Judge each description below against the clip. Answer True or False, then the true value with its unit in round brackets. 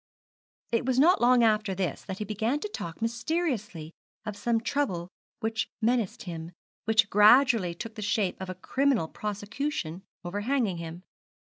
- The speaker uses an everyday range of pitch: True (4.7 semitones)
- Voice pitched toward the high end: True (215 Hz)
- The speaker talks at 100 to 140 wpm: False (150 wpm)